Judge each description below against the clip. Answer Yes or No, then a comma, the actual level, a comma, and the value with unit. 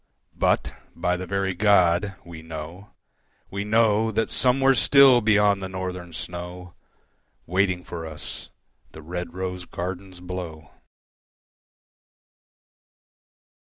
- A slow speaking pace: Yes, slow, 105 wpm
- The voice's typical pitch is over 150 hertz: No, very low, 90 Hz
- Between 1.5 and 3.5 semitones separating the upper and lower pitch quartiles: Yes, average, 2.8 semitones